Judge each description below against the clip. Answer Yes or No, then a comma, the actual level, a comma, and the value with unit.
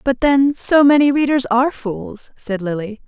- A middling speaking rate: Yes, average, 175 wpm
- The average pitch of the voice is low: No, very high, 255 Hz